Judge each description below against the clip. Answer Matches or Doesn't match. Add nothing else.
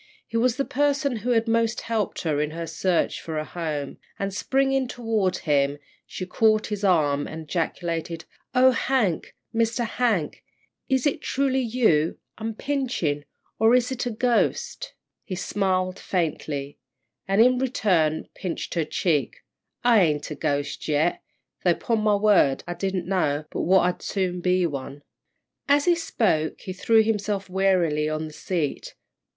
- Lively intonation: Matches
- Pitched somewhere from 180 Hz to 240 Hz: Matches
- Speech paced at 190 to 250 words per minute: Doesn't match